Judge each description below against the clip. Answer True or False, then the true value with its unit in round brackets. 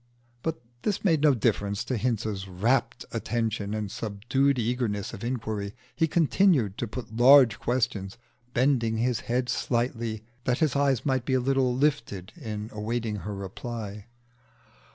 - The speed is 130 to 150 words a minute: True (145 wpm)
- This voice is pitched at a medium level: False (120 Hz)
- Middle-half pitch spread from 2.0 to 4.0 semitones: True (3.7 semitones)